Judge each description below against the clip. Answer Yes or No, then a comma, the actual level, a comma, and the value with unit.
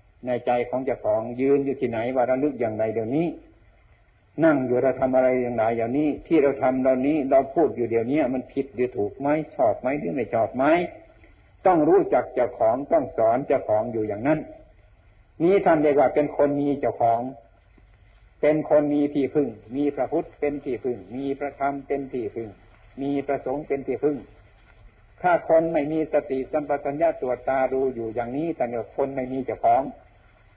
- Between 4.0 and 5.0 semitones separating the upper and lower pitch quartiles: Yes, average, 4.6 semitones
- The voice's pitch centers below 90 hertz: No, low, 130 Hz